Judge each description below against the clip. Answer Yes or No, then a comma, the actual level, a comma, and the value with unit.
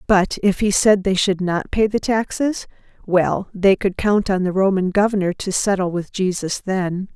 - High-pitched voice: Yes, high, 195 Hz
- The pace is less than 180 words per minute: No, average, 185 wpm